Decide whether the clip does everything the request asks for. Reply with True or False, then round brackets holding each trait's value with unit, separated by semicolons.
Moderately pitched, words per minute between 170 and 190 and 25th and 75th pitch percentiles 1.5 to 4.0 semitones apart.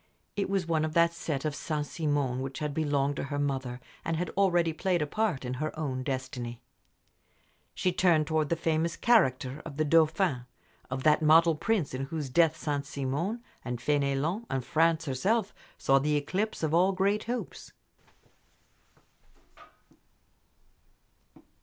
False (155 Hz; 155 wpm; 3.6 semitones)